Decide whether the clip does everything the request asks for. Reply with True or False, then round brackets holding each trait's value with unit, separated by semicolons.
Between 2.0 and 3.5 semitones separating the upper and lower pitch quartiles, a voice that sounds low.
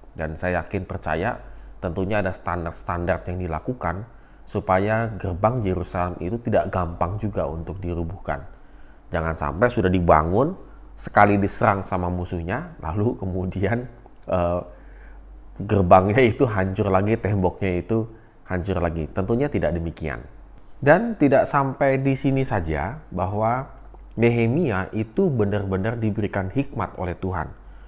False (4.3 semitones; 95 Hz)